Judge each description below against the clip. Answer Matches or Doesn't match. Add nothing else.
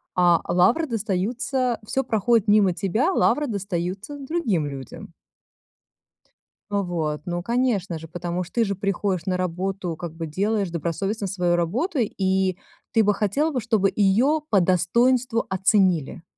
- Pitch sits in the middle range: Doesn't match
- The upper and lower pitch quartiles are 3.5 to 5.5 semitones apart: Matches